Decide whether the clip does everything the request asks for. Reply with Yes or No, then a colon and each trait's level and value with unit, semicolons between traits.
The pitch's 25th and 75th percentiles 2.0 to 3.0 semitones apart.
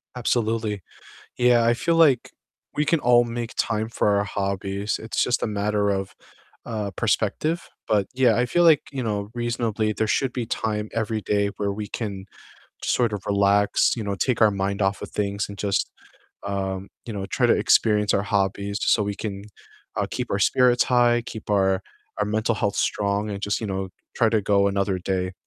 Yes: average, 2.7 semitones